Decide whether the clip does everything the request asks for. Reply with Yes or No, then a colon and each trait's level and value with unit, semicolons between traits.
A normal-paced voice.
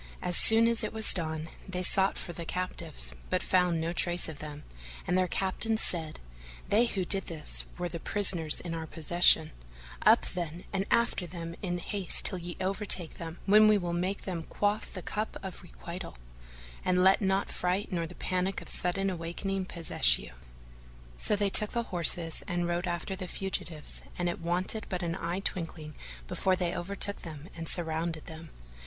Yes: average, 185 wpm